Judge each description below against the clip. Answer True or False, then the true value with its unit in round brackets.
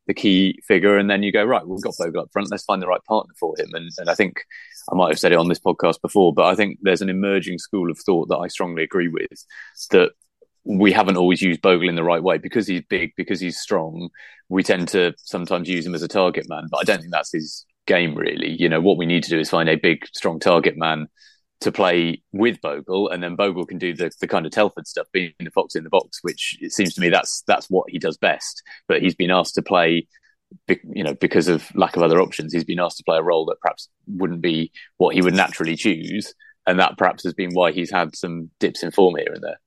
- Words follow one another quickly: True (260 wpm)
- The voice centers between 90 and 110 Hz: True (95 Hz)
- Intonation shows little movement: False (3.0 semitones)